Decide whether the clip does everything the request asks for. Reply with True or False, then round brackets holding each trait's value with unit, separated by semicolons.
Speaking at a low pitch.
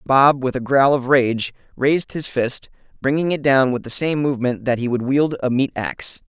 True (130 Hz)